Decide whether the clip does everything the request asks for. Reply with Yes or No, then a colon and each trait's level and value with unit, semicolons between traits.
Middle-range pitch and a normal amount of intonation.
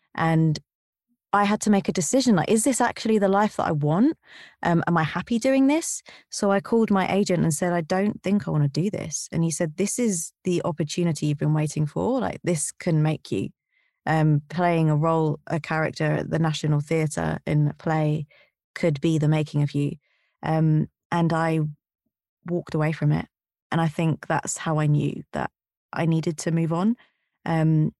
Yes: medium, 165 Hz; average, 4.1 semitones